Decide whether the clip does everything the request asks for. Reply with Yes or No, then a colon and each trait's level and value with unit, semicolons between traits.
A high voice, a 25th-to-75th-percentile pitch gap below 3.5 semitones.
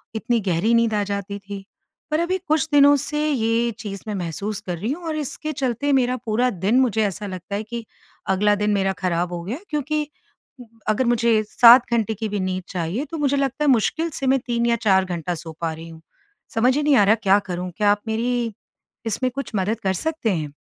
No: high, 220 Hz; average, 5.0 semitones